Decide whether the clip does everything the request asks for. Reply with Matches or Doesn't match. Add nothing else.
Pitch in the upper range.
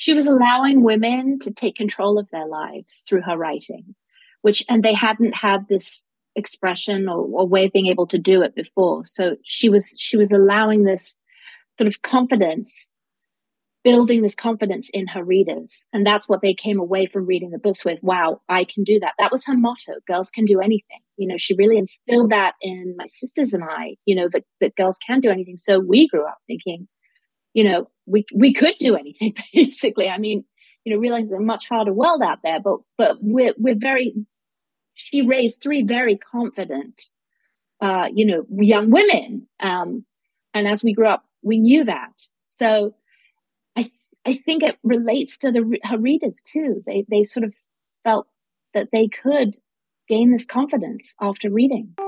Matches